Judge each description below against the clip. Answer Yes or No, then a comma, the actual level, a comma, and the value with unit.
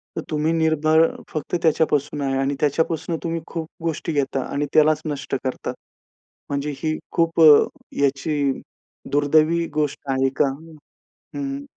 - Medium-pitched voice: Yes, medium, 155 Hz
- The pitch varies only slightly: Yes, narrow, 2.2 semitones